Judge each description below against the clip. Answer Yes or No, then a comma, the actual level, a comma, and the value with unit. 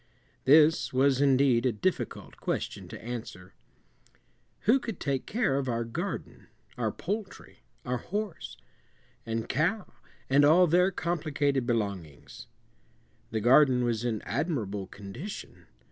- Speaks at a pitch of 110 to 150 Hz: Yes, low, 135 Hz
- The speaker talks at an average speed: No, slow, 120 wpm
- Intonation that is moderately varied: No, wide, 6.5 semitones